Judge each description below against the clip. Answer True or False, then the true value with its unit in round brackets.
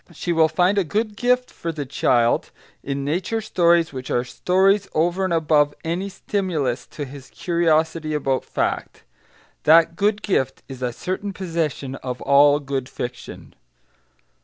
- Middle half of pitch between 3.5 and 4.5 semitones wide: False (5.1 semitones)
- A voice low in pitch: False (160 Hz)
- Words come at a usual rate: True (150 wpm)